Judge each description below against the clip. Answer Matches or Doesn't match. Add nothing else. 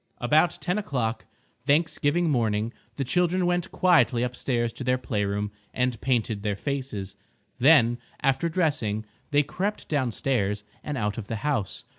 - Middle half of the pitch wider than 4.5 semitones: Matches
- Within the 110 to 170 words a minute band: Matches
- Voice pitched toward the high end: Doesn't match